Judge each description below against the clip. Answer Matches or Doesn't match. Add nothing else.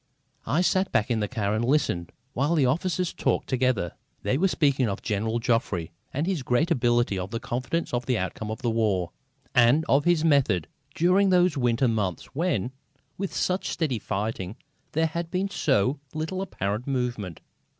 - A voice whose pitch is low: Matches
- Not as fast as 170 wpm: Doesn't match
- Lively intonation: Matches